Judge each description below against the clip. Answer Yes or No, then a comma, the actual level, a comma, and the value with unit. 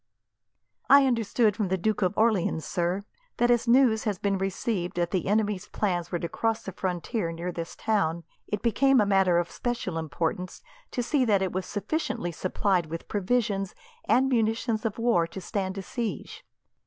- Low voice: No, high, 200 Hz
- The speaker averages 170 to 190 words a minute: Yes, average, 180 wpm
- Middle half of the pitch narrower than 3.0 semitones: No, average, 4.2 semitones